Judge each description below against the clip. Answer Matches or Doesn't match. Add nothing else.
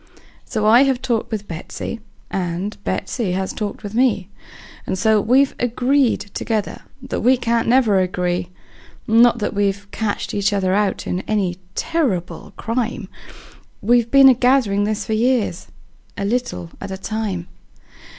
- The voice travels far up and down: Doesn't match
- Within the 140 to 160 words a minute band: Matches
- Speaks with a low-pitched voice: Doesn't match